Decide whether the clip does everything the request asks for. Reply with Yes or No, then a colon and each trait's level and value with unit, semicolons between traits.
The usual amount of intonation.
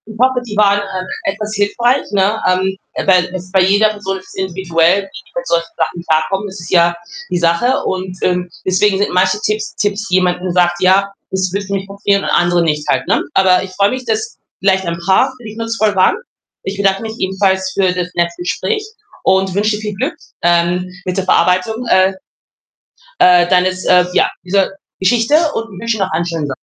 No: narrow, 2.3 semitones